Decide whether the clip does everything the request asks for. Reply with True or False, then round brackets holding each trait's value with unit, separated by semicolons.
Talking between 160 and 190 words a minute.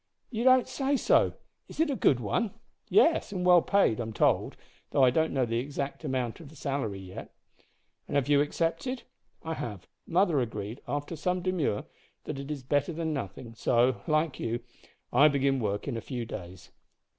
True (185 wpm)